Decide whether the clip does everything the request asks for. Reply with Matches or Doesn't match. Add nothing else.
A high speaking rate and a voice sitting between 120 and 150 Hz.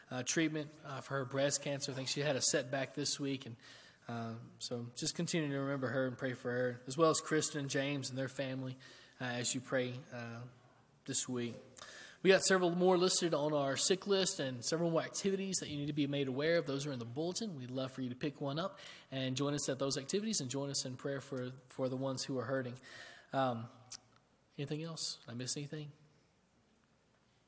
Matches